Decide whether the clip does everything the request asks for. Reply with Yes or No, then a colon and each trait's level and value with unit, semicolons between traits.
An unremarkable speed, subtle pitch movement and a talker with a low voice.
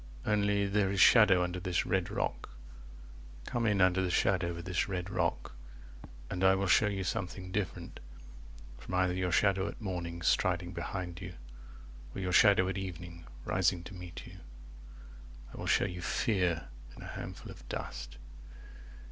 Yes: average, 165 wpm; narrow, 1.8 semitones; very low, 90 Hz